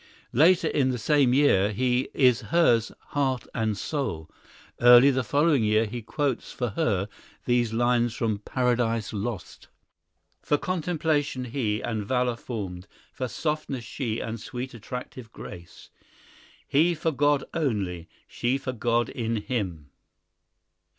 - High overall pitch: No, low, 120 Hz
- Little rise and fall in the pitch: No, average, 4.0 semitones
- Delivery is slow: Yes, slow, 130 wpm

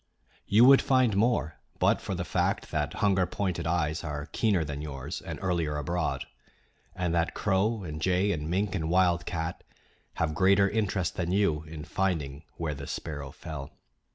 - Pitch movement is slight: No, average, 4.2 semitones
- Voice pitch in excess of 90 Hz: No, very low, 85 Hz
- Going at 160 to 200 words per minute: Yes, average, 165 wpm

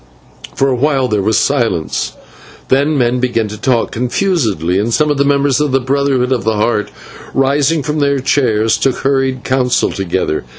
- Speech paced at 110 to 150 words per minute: No, average, 175 wpm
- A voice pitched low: Yes, low, 130 Hz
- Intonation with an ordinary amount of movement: Yes, average, 3.8 semitones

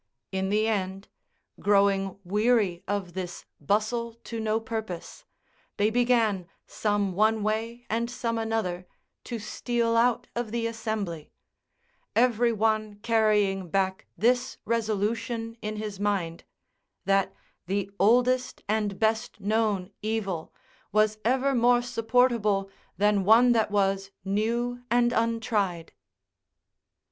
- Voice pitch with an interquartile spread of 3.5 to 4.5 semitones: No, average, 2.7 semitones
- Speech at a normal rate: No, slow, 115 wpm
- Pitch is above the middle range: Yes, high, 215 Hz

